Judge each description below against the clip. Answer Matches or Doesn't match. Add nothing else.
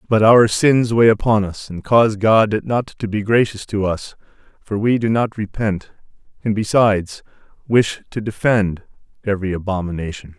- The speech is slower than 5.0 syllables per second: Matches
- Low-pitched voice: Matches